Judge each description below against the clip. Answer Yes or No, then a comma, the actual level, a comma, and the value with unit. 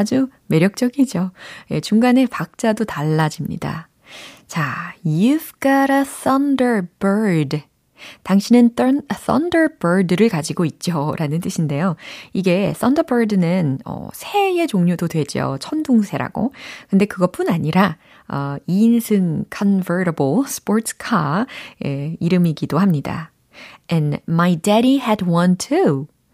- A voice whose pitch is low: No, high, 195 Hz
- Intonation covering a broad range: Yes, wide, 6.4 semitones